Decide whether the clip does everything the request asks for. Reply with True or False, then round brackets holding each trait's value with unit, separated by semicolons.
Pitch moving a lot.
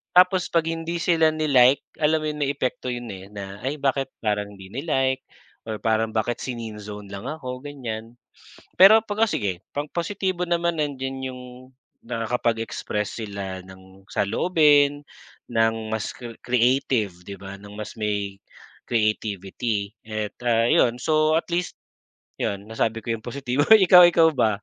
True (6.3 semitones)